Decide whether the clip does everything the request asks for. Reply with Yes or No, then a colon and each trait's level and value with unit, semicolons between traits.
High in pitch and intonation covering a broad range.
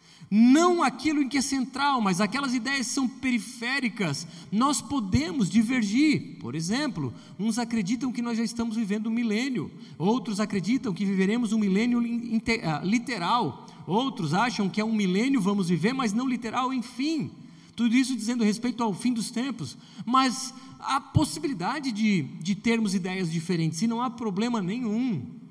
No: high, 230 Hz; average, 4.0 semitones